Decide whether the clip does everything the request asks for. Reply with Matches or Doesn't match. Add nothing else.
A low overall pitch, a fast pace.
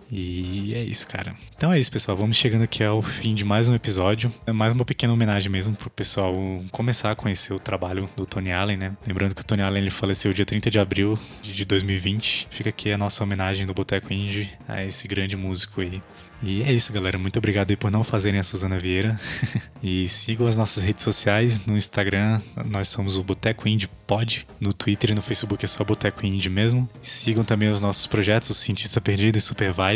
Matches